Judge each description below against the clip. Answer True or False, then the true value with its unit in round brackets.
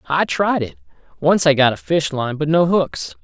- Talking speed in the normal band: False (225 wpm)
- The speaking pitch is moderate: True (150 Hz)